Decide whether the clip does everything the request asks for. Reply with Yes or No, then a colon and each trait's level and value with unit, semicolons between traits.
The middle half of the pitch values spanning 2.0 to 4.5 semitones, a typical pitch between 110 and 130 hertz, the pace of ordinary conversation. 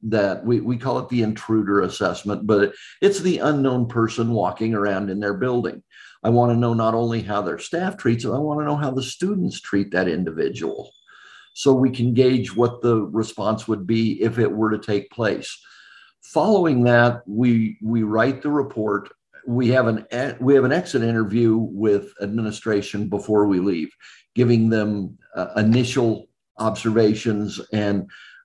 Yes: narrow, 2.6 semitones; low, 115 Hz; average, 170 wpm